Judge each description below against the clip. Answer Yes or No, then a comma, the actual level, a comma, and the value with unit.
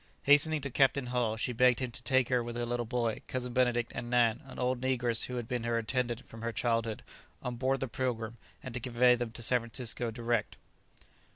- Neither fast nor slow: No, fast, 215 wpm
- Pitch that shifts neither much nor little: No, narrow, 1.5 semitones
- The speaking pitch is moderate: No, low, 120 Hz